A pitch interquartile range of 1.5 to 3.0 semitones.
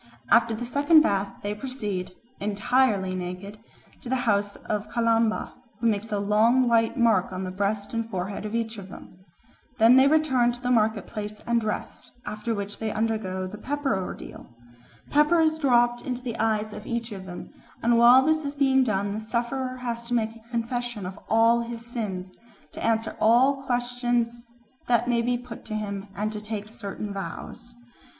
Yes: average, 2.7 semitones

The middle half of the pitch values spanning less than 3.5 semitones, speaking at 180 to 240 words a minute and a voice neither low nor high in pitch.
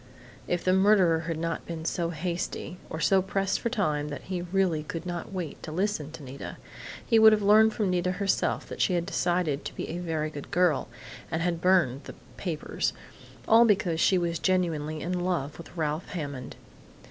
Yes: average, 2.8 semitones; average, 195 wpm; medium, 175 Hz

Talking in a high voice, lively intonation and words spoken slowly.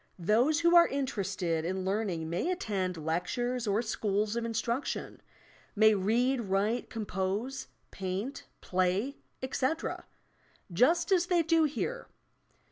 Yes: high, 220 Hz; wide, 5.9 semitones; slow, 120 wpm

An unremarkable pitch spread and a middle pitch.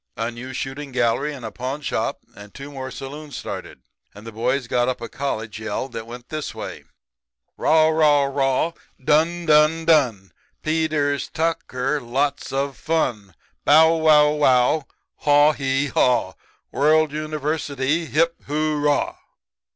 Yes: average, 3.3 semitones; medium, 145 Hz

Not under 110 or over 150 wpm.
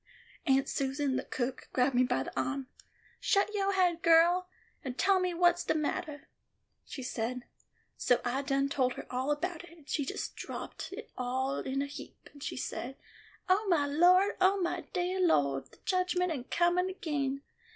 No: average, 180 wpm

